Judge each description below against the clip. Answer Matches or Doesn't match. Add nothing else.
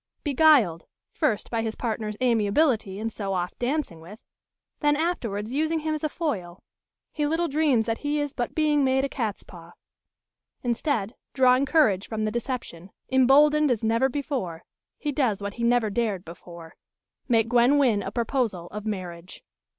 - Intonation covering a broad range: Matches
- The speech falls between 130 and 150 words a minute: Doesn't match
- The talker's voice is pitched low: Doesn't match